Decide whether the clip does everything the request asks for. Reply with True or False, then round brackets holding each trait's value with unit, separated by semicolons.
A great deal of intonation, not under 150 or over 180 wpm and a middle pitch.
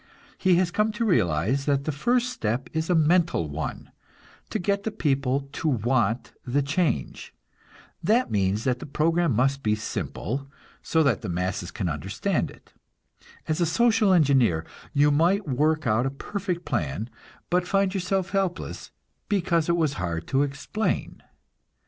True (7.1 semitones; 155 wpm; 145 Hz)